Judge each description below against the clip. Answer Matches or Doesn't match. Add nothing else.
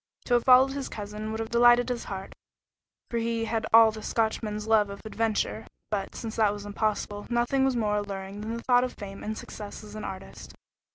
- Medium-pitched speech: Doesn't match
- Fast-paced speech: Matches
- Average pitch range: Doesn't match